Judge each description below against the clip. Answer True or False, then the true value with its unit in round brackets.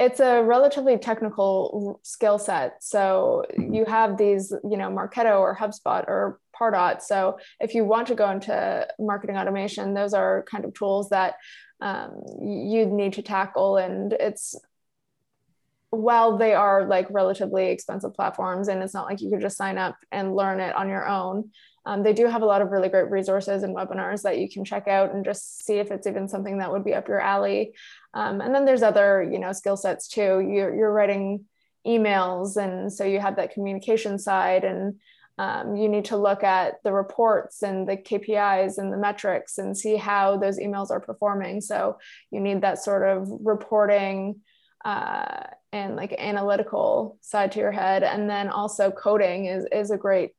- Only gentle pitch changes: True (1.5 semitones)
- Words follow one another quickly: False (185 wpm)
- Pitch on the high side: True (200 Hz)